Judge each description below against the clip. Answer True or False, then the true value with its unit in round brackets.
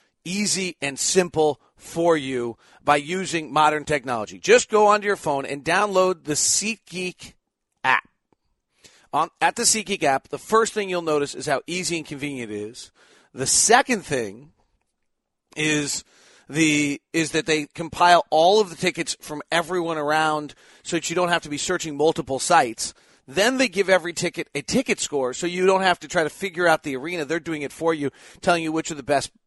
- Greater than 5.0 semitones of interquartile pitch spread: False (3.8 semitones)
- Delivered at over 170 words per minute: True (185 wpm)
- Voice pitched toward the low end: False (165 Hz)